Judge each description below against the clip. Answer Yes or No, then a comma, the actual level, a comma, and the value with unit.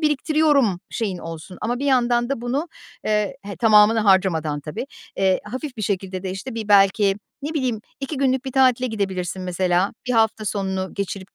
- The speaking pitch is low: No, high, 210 Hz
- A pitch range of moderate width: Yes, average, 5.0 semitones